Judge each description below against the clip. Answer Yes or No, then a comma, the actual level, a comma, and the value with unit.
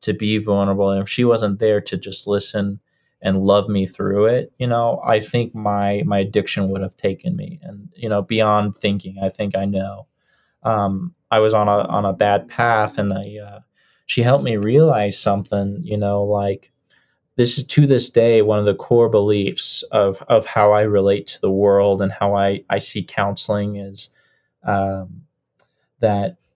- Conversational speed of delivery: Yes, average, 190 wpm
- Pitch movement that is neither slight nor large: No, narrow, 1.9 semitones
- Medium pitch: No, low, 105 Hz